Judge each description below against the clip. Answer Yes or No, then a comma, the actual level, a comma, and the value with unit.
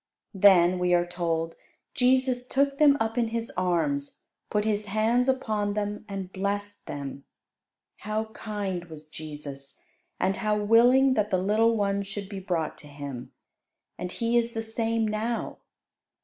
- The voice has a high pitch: Yes, high, 205 Hz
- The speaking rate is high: No, average, 150 wpm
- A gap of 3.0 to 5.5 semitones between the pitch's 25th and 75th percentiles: Yes, average, 4.3 semitones